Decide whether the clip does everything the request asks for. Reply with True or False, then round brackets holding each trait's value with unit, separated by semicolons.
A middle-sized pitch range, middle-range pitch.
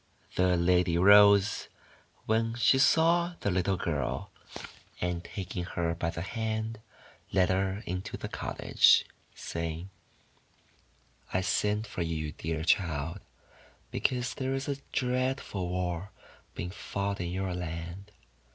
False (4.2 semitones; 95 Hz)